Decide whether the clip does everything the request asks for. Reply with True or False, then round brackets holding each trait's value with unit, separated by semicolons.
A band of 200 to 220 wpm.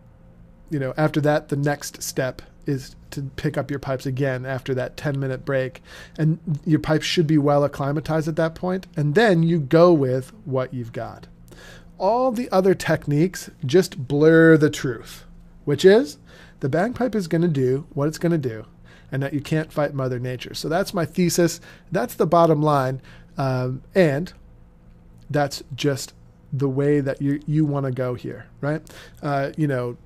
False (180 wpm)